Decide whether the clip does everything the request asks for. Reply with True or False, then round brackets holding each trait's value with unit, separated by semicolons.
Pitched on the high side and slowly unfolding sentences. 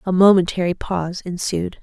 False (180 Hz; 130 wpm)